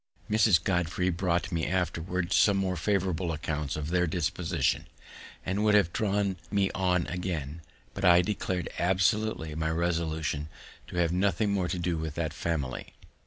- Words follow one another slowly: No, average, 155 wpm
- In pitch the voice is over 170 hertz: No, very low, 90 Hz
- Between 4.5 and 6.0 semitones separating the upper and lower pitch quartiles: No, average, 2.7 semitones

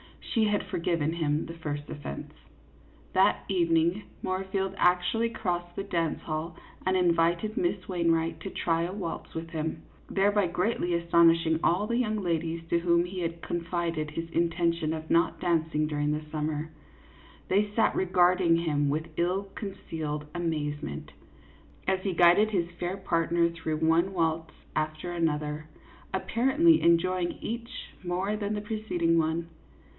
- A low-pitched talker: No, medium, 170 Hz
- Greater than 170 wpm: No, average, 145 wpm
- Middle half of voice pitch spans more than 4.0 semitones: No, narrow, 2.6 semitones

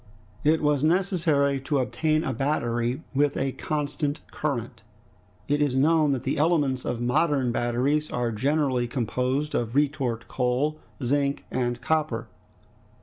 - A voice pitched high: No, medium, 140 Hz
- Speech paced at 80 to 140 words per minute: Yes, slow, 135 wpm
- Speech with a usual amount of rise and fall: Yes, average, 3.4 semitones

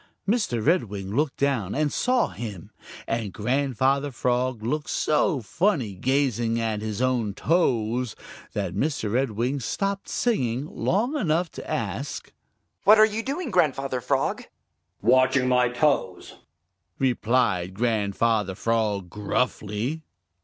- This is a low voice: Yes, low, 125 Hz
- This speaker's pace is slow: Yes, slow, 115 wpm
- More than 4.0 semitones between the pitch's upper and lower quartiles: Yes, average, 5.3 semitones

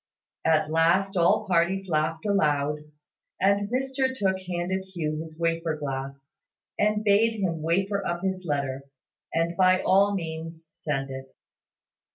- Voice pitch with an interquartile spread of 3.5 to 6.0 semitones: Yes, average, 3.9 semitones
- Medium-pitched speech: Yes, medium, 170 Hz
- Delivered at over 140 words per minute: No, slow, 135 wpm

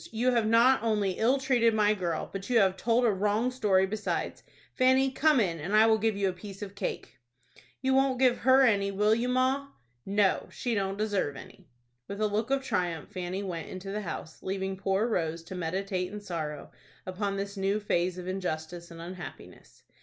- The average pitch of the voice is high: Yes, high, 200 Hz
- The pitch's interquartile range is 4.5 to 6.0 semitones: No, average, 3.7 semitones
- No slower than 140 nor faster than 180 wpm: No, average, 200 wpm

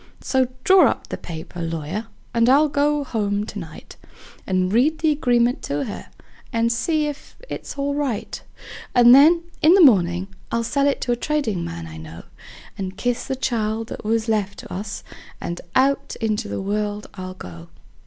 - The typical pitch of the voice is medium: No, high, 230 Hz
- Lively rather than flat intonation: Yes, wide, 6.5 semitones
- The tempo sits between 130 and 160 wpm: No, average, 175 wpm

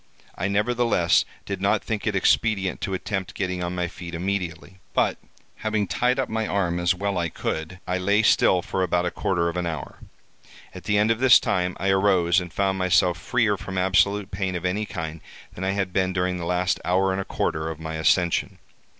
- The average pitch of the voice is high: No, very low, 95 Hz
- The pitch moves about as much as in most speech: No, narrow, 2.3 semitones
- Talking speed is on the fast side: Yes, fast, 210 wpm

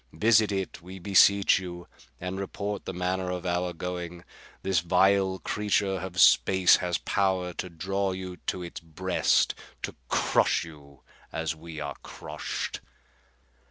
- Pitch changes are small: Yes, narrow, 1.7 semitones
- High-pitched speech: No, very low, 90 Hz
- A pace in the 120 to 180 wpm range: Yes, average, 140 wpm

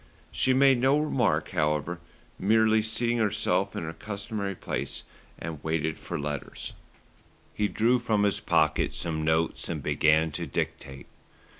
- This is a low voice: Yes, low, 100 Hz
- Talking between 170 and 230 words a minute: No, average, 140 wpm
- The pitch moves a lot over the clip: Yes, wide, 5.9 semitones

